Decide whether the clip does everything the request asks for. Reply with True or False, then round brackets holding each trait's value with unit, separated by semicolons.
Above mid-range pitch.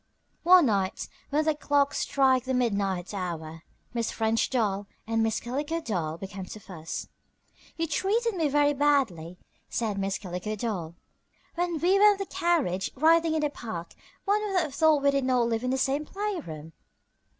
True (255 Hz)